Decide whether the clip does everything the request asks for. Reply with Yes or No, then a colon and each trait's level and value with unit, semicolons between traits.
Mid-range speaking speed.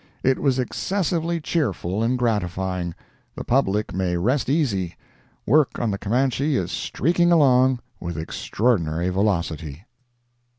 No: slow, 115 wpm